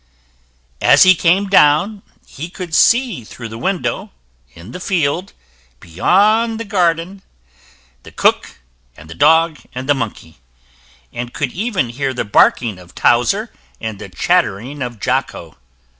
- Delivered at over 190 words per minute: No, average, 145 wpm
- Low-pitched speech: No, medium, 145 Hz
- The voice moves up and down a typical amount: No, wide, 8.6 semitones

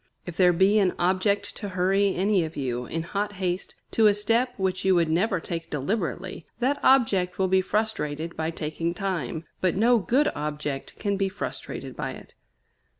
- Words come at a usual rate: Yes, average, 180 wpm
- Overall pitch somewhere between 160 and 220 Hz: Yes, medium, 185 Hz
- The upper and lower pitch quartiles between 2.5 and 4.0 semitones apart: Yes, average, 3.6 semitones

